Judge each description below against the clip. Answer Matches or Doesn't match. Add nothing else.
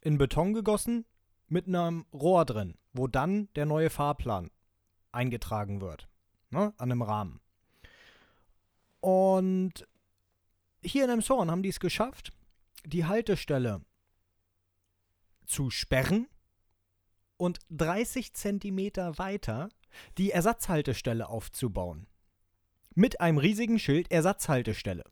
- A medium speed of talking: Doesn't match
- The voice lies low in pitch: Matches